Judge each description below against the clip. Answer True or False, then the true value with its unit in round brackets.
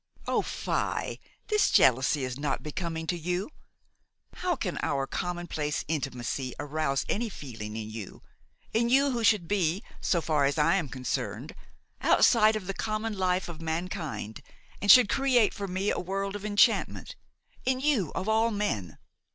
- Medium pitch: True (180 Hz)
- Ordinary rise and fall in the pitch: False (6.6 semitones)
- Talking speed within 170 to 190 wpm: False (155 wpm)